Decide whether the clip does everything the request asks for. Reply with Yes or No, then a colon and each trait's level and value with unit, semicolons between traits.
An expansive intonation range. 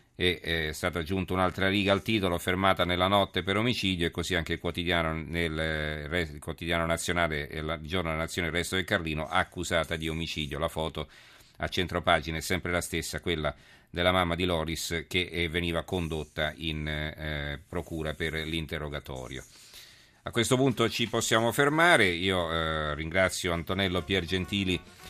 No: average, 2.7 semitones